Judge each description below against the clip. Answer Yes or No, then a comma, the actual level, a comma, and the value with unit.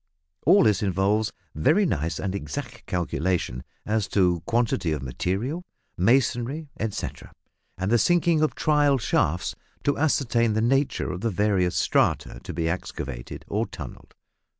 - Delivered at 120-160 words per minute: Yes, average, 140 wpm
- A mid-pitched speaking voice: No, low, 105 Hz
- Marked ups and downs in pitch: Yes, wide, 7.2 semitones